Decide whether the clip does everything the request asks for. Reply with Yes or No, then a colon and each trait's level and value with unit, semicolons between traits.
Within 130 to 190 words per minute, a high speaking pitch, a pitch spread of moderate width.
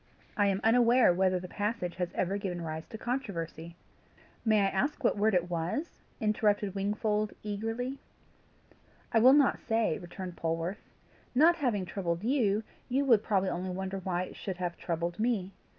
Yes: average, 165 wpm; high, 200 Hz; average, 4.0 semitones